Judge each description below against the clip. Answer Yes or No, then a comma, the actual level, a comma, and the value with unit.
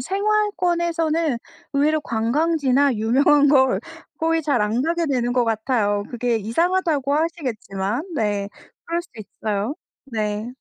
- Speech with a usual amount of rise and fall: No, wide, 6.5 semitones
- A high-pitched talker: Yes, very high, 270 Hz